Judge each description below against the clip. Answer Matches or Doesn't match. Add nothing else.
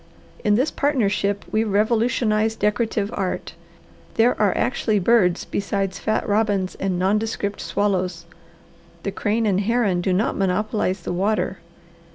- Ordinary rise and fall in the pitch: Doesn't match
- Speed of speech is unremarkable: Doesn't match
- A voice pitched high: Matches